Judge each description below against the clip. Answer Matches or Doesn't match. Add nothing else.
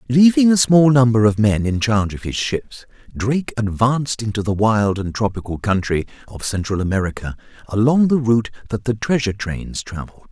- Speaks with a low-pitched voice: Matches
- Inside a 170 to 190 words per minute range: Matches